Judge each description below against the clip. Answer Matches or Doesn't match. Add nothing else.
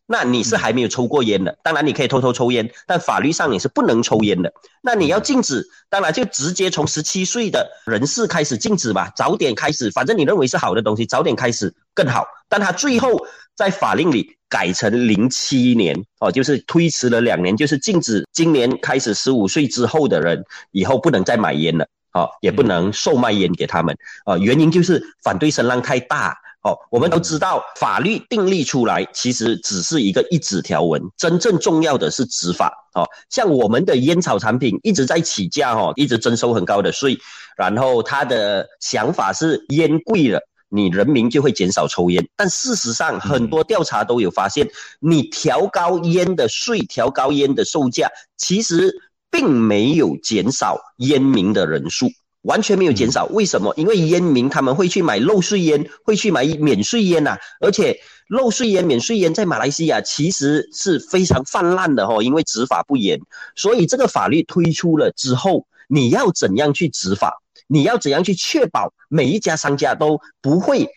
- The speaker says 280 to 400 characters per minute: Matches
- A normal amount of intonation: Doesn't match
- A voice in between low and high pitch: Matches